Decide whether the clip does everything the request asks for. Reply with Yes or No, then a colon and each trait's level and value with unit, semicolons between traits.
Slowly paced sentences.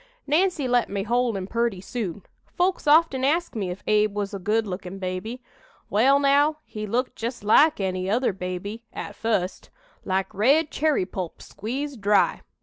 No: average, 165 wpm